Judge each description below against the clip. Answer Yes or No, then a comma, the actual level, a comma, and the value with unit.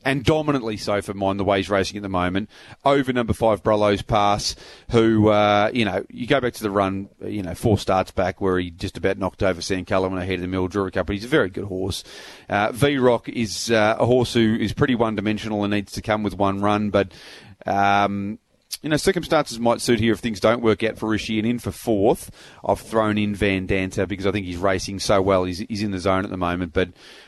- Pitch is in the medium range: No, low, 105 Hz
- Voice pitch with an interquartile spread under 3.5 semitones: Yes, narrow, 2.6 semitones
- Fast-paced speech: Yes, fast, 245 wpm